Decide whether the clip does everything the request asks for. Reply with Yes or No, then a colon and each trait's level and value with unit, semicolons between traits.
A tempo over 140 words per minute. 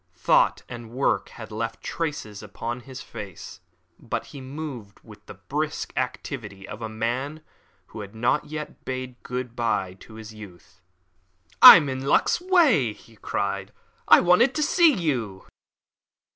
Yes: average, 150 wpm